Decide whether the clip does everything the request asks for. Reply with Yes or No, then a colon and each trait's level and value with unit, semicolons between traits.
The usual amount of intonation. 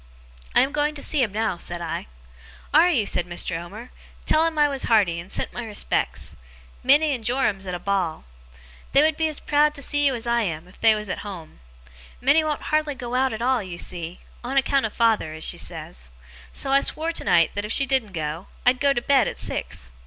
No: wide, 7.3 semitones